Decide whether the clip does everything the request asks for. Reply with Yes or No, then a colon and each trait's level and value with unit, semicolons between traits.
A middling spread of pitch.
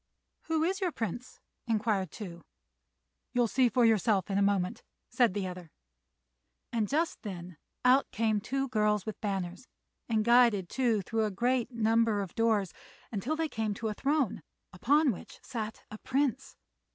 Yes: average, 3.8 semitones